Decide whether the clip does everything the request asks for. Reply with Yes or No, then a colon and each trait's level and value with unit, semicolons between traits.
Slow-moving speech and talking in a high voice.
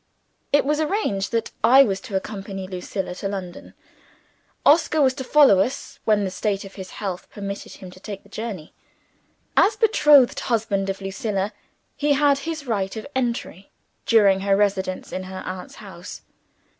No: average, 165 wpm; high, 200 Hz